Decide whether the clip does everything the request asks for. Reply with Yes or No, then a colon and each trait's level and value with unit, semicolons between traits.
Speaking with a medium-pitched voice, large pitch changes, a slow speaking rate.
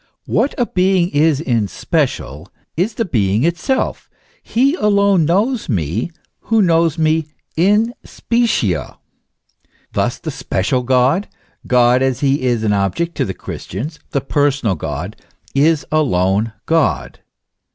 Yes: medium, 145 Hz; wide, 8.0 semitones; slow, 130 wpm